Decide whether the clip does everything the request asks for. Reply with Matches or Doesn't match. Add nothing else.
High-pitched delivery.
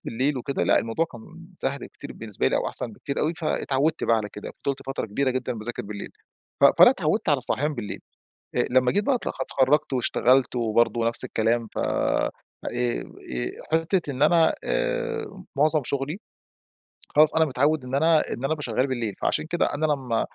Doesn't match